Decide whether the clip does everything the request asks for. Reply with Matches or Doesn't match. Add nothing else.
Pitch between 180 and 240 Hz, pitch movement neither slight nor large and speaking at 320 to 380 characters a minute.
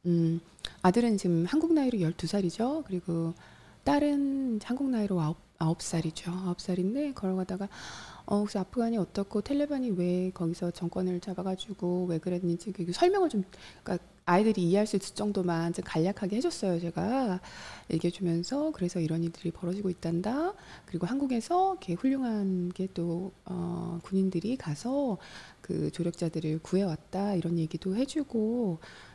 Matches